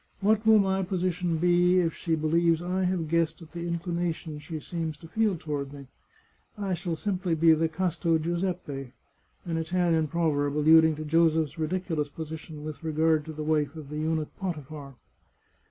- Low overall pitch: No, medium, 165 Hz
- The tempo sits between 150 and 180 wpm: Yes, average, 170 wpm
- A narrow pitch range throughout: Yes, narrow, 2.3 semitones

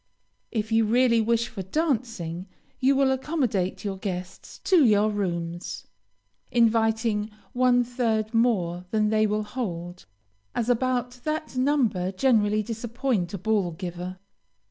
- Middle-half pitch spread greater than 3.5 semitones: Yes, average, 4.5 semitones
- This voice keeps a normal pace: No, slow, 125 wpm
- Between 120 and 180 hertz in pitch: No, high, 220 Hz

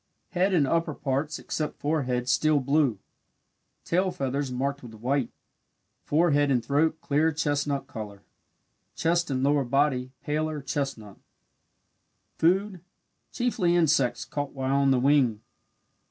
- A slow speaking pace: Yes, slow, 125 wpm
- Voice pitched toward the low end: No, medium, 145 Hz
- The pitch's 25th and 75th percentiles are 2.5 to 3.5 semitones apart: Yes, average, 3.1 semitones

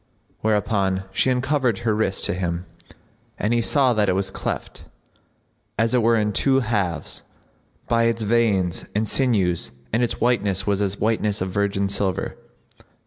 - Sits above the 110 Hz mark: No, low, 105 Hz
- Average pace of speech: Yes, average, 160 wpm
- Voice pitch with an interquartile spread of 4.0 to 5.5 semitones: No, average, 3.2 semitones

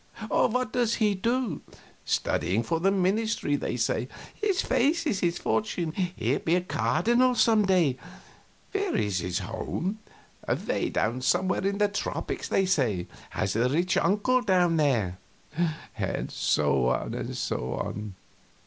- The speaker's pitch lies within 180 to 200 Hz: Yes, medium, 185 Hz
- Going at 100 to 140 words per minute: Yes, slow, 135 wpm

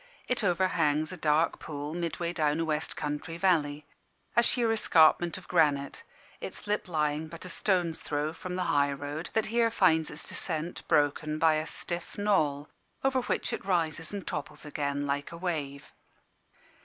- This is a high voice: No, medium, 160 Hz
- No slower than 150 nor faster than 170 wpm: Yes, average, 165 wpm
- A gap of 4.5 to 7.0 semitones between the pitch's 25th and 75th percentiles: No, average, 3.4 semitones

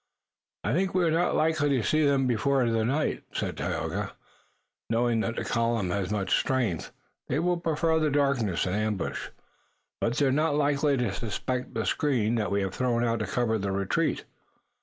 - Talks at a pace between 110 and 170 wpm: No, average, 180 wpm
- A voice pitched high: No, low, 120 Hz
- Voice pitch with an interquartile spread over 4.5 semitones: Yes, average, 5.2 semitones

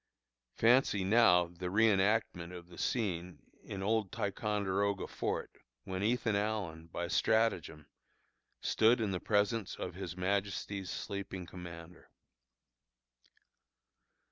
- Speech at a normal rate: No, slow, 105 wpm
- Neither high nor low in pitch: No, low, 100 Hz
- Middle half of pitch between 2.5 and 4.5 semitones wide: Yes, average, 3.4 semitones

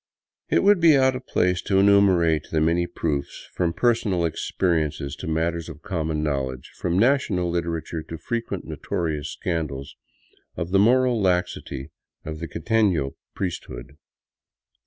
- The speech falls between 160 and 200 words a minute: No, average, 145 wpm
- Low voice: Yes, very low, 85 Hz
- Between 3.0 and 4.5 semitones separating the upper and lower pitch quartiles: Yes, average, 4.2 semitones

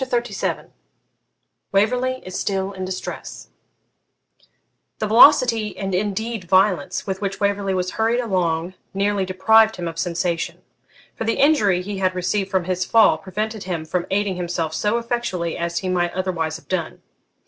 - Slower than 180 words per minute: Yes, average, 155 wpm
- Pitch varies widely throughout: No, average, 3.1 semitones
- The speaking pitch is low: No, high, 190 Hz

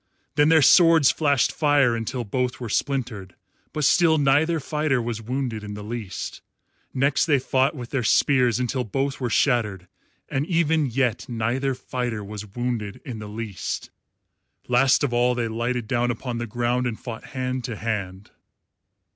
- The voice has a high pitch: No, low, 125 Hz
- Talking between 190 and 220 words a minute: No, average, 165 wpm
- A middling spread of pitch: Yes, average, 3.3 semitones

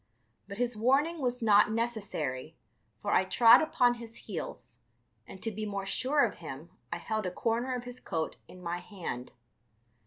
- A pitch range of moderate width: Yes, average, 5.0 semitones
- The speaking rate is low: No, average, 175 wpm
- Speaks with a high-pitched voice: Yes, high, 220 Hz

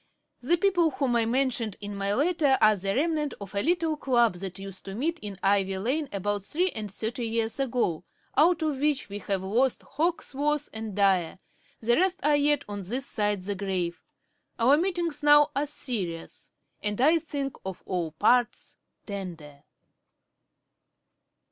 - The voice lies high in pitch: Yes, high, 235 Hz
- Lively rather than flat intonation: Yes, wide, 6.8 semitones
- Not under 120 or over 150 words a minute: No, average, 160 wpm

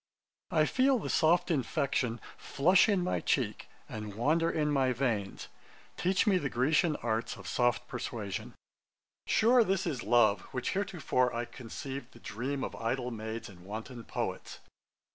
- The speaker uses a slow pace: No, average, 150 wpm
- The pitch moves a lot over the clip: Yes, wide, 6.2 semitones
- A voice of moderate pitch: No, low, 130 Hz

